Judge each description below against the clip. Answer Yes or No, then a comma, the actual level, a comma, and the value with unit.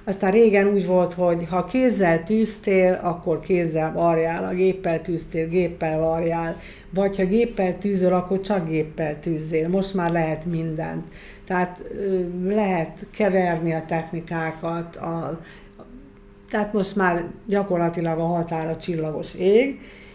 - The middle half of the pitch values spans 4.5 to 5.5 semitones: No, average, 2.8 semitones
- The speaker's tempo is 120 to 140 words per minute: Yes, average, 125 wpm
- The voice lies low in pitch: No, medium, 175 Hz